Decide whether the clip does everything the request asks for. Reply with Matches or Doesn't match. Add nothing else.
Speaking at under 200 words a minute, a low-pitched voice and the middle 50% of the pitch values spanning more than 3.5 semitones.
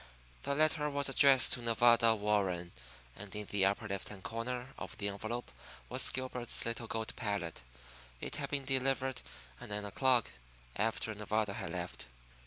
Matches